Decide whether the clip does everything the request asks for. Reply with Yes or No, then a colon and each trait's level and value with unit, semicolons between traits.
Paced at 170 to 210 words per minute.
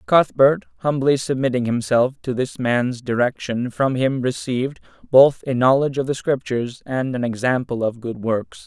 No: average, 160 wpm